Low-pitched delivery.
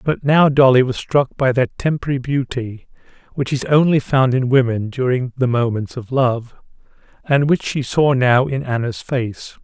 Yes: low, 130 Hz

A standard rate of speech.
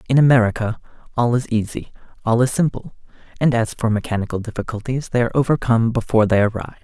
Yes: average, 165 wpm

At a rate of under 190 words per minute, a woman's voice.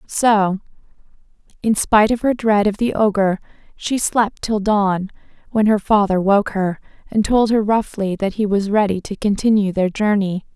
Yes: average, 170 wpm; female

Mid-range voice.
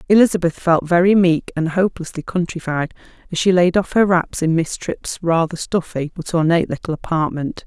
Yes: medium, 170 Hz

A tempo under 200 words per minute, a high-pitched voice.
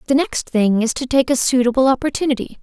No: fast, 205 wpm; very high, 255 Hz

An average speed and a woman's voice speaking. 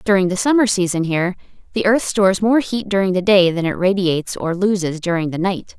No: fast, 220 wpm; female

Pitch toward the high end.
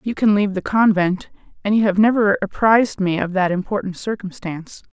Yes: high, 200 Hz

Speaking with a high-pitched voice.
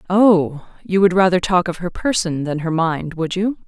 No: medium, 180 Hz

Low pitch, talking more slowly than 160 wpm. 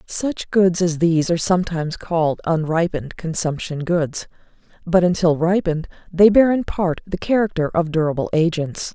No: medium, 170 Hz; average, 150 wpm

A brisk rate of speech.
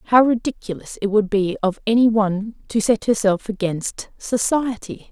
No: average, 155 wpm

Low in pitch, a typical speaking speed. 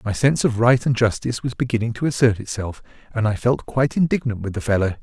No: low, 115 Hz; fast, 225 wpm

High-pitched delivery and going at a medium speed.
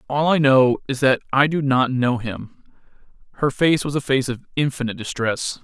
No: low, 135 Hz; average, 190 wpm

